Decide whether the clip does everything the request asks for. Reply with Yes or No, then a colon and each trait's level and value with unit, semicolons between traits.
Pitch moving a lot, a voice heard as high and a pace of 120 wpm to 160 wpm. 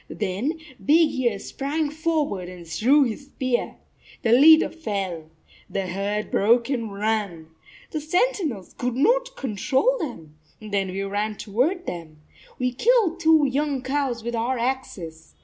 Yes: wide, 7.1 semitones; high, 245 Hz; average, 145 wpm